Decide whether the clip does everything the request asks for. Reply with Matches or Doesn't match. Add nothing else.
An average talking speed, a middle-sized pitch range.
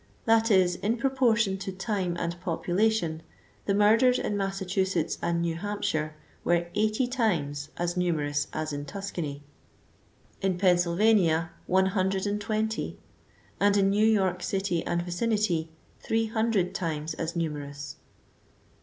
Doesn't match